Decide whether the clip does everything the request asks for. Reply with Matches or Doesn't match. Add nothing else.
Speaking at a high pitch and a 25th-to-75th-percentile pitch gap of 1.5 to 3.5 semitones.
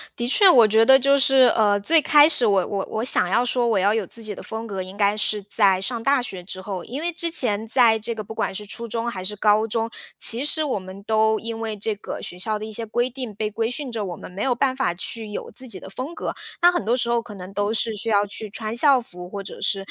Matches